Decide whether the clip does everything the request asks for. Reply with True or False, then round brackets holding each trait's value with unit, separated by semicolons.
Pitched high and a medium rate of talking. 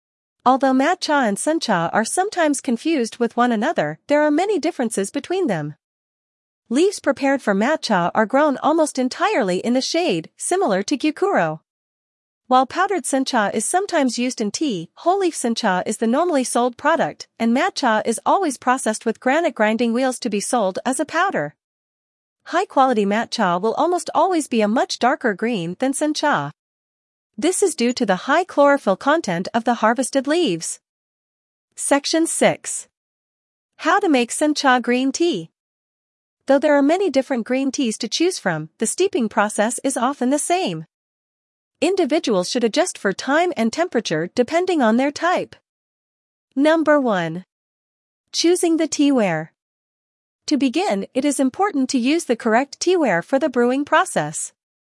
True (265 Hz; 155 wpm)